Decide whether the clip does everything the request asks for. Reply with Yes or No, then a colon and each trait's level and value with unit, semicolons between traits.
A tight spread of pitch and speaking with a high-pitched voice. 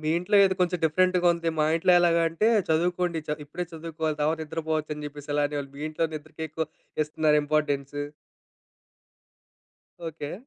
No: narrow, 2.0 semitones; medium, 160 Hz